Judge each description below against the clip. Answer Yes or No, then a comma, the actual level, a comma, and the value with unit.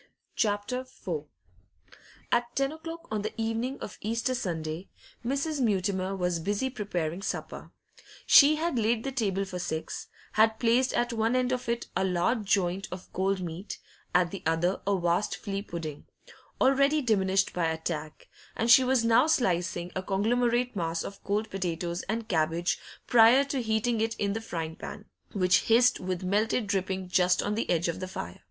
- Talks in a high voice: Yes, high, 205 Hz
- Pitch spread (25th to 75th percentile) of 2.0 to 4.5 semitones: No, average, 4.9 semitones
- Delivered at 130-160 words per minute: No, average, 170 wpm